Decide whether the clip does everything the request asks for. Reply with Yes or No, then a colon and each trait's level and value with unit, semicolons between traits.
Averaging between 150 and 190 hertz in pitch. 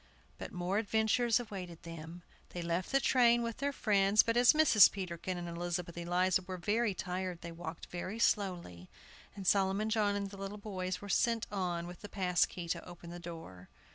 Yes: medium, 185 Hz